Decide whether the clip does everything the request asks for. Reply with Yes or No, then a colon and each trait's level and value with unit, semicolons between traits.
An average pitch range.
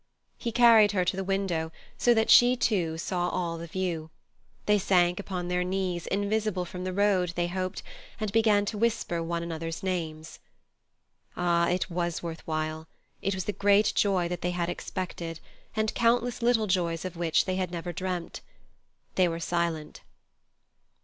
Yes: average, 3.0 semitones